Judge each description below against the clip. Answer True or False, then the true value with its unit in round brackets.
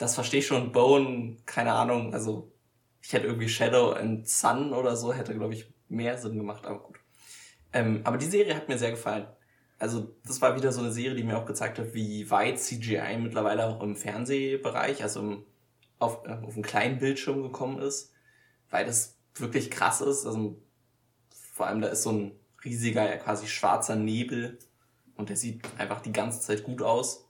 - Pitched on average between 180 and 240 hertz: False (115 Hz)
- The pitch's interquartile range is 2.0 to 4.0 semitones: True (2.7 semitones)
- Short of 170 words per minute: False (185 wpm)